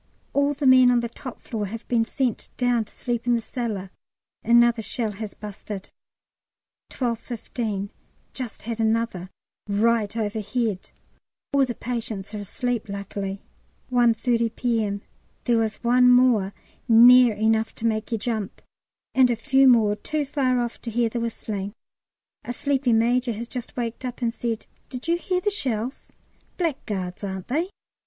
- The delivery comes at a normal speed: Yes, average, 155 wpm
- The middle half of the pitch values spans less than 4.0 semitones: Yes, narrow, 2.5 semitones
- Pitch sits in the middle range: No, high, 235 Hz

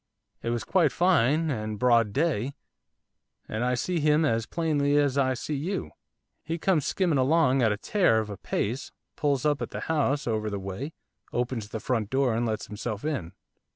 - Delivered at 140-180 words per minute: No, average, 190 wpm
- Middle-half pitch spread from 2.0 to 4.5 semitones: No, wide, 5.4 semitones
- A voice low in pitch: Yes, low, 130 Hz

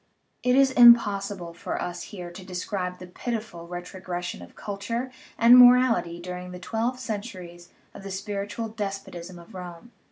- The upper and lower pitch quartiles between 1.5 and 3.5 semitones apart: No, average, 4.4 semitones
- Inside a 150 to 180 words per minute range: Yes, average, 155 wpm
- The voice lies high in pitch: Yes, high, 195 Hz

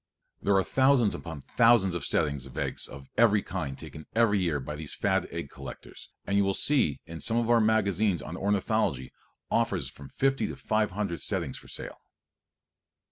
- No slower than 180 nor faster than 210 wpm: Yes, average, 190 wpm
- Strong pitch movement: Yes, wide, 6.1 semitones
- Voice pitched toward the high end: No, low, 100 Hz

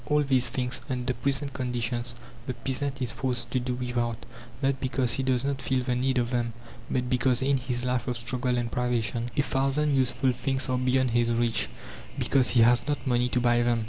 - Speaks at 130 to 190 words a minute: No, fast, 205 wpm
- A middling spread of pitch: No, narrow, 1.6 semitones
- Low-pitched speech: Yes, low, 125 Hz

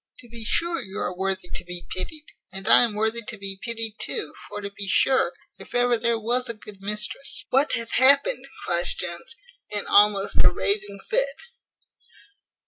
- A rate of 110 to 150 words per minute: No, average, 185 wpm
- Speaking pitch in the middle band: No, high, 215 Hz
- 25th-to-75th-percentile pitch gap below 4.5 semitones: Yes, average, 3.8 semitones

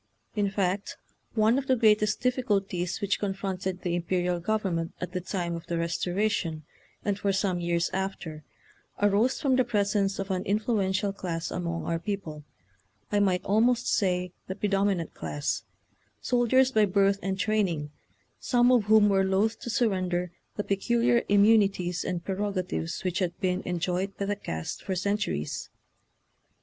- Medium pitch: No, high, 195 Hz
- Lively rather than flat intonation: No, average, 2.8 semitones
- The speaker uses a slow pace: No, average, 160 wpm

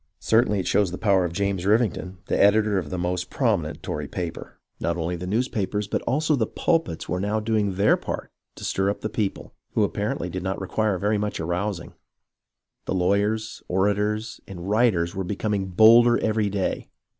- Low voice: Yes, low, 100 Hz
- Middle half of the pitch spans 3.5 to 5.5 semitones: No, average, 3.0 semitones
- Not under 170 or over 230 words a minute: Yes, average, 180 wpm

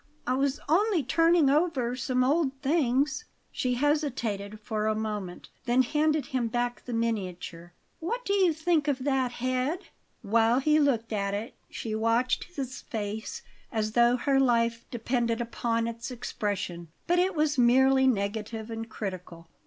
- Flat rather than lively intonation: No, average, 4.5 semitones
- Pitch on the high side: Yes, high, 245 Hz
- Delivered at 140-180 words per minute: Yes, average, 155 wpm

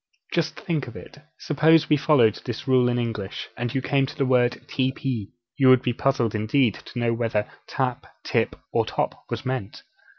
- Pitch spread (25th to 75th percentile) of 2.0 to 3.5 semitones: Yes, average, 2.7 semitones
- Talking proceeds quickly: No, average, 190 wpm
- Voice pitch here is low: Yes, low, 125 Hz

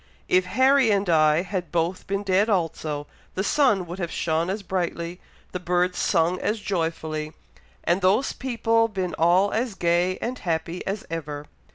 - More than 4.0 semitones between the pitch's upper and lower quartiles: No, average, 3.2 semitones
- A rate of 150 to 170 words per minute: Yes, average, 165 wpm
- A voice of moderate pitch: Yes, medium, 180 Hz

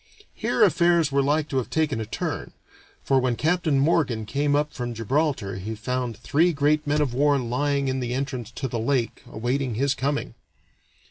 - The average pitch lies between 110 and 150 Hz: Yes, low, 135 Hz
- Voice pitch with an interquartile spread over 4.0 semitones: No, average, 3.3 semitones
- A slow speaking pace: No, average, 185 wpm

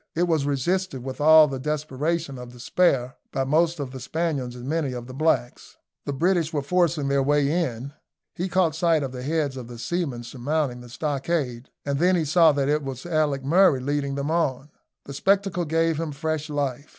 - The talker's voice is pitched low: No, medium, 145 Hz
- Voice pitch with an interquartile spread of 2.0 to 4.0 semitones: Yes, average, 3.6 semitones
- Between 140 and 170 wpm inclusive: No, average, 200 wpm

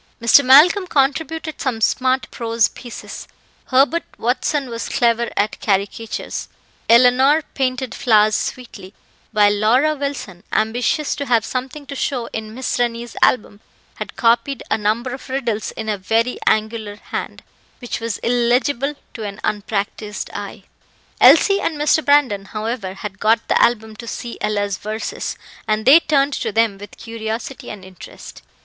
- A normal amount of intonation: Yes, average, 3.7 semitones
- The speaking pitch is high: Yes, high, 235 Hz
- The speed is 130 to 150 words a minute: Yes, average, 145 wpm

